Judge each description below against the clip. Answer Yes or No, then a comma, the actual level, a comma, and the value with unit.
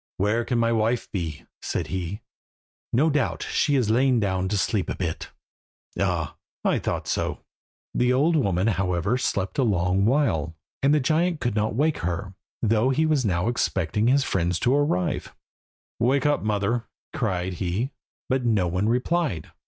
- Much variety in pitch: Yes, wide, 5.9 semitones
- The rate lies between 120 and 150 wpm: No, average, 165 wpm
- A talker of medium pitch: No, low, 110 Hz